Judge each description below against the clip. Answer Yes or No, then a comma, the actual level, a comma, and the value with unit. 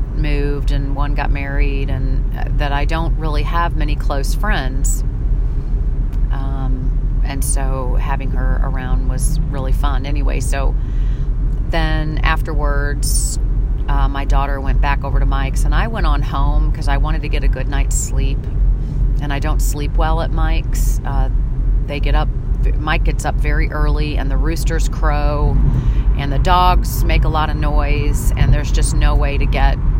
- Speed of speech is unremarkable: Yes, average, 170 wpm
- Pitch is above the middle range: No, medium, 140 Hz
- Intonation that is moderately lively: No, narrow, 2.2 semitones